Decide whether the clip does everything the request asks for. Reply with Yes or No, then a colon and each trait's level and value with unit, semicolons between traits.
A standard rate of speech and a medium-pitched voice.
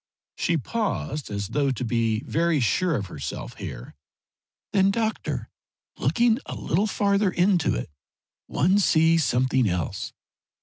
No: slow, 130 wpm; medium, 155 Hz